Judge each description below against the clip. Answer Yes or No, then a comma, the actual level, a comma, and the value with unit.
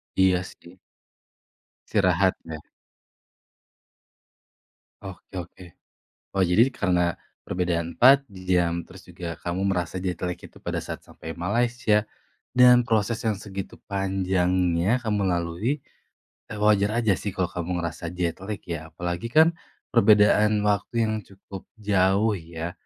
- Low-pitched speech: Yes, very low, 95 Hz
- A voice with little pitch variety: No, average, 3.3 semitones